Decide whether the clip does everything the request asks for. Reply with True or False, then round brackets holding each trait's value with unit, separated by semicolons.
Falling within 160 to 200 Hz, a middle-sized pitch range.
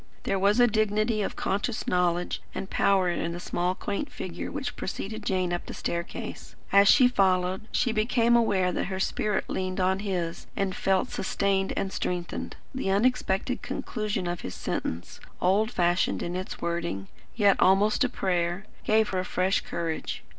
True (190 Hz; 3.1 semitones)